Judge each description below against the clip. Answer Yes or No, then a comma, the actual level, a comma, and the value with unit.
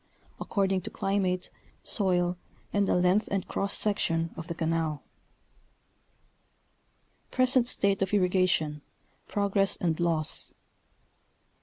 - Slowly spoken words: Yes, slow, 100 wpm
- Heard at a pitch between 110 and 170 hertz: No, medium, 185 Hz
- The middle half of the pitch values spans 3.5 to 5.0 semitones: No, average, 3.1 semitones